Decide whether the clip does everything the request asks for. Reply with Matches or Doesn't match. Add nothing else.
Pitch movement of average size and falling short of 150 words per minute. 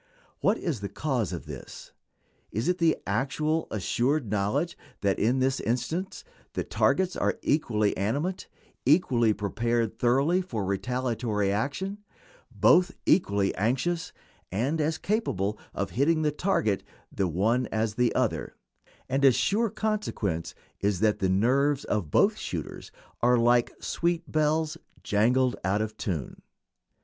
Doesn't match